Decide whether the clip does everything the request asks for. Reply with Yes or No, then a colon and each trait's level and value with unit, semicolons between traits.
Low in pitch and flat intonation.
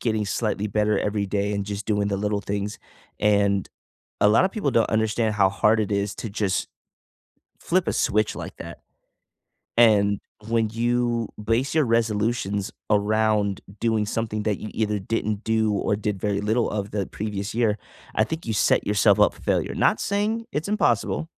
Yes: low, 105 Hz; narrow, 1.9 semitones